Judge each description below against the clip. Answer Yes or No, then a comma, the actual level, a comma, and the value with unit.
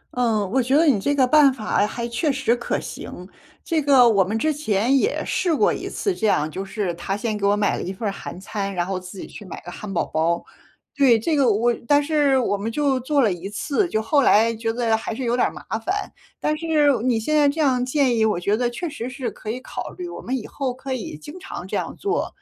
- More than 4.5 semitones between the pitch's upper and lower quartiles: Yes, wide, 5.5 semitones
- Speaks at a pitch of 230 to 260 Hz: Yes, high, 240 Hz